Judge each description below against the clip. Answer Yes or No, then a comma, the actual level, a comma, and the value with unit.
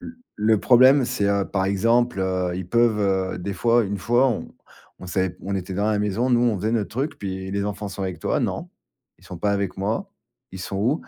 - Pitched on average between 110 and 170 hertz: No, low, 100 Hz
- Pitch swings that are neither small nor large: Yes, average, 3.6 semitones